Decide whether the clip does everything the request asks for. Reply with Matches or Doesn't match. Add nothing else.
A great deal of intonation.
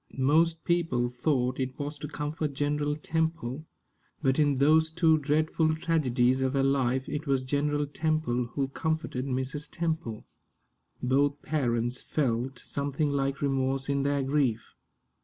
Doesn't match